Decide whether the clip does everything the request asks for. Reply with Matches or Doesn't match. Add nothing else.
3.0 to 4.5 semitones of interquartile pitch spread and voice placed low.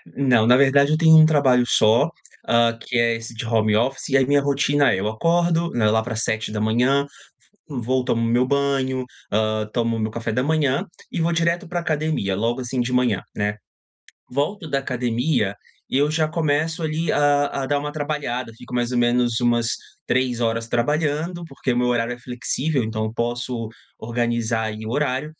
Matches